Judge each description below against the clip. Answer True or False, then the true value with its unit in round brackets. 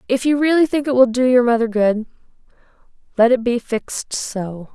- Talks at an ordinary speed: True (190 wpm)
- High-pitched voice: True (245 Hz)